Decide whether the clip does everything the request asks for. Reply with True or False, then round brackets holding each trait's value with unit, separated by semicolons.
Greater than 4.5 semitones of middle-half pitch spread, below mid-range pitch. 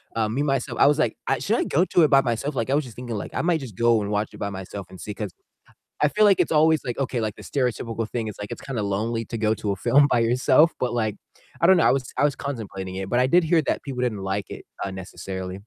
True (5.2 semitones; 120 Hz)